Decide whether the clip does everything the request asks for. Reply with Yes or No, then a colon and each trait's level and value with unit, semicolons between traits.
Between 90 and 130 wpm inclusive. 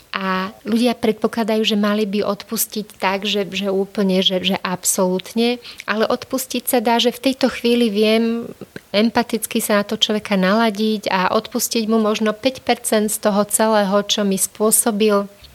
No: average, 155 wpm